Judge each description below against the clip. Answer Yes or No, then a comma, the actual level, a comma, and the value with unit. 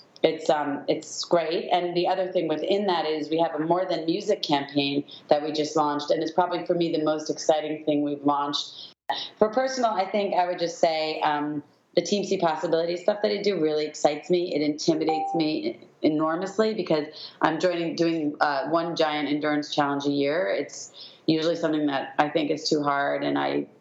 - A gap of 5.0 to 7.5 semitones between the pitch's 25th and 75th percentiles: No, average, 2.9 semitones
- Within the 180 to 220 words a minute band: Yes, average, 200 wpm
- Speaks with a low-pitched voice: No, medium, 160 Hz